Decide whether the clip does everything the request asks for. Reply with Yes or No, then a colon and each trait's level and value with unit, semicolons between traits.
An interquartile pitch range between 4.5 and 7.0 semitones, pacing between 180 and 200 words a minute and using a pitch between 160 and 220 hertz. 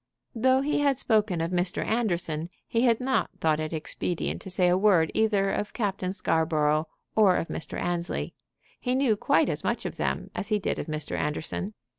Yes: average, 5.1 semitones; average, 190 wpm; high, 190 Hz